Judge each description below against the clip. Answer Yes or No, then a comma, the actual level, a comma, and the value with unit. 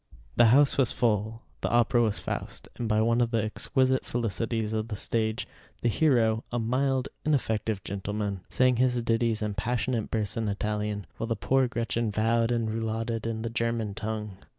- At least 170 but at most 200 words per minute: Yes, average, 175 wpm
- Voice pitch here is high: No, low, 115 Hz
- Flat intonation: Yes, narrow, 1.8 semitones